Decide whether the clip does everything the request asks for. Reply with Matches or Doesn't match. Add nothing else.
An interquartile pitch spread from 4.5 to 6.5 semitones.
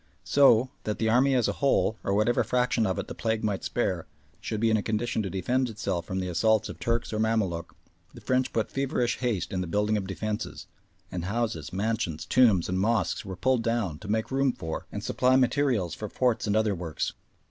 Doesn't match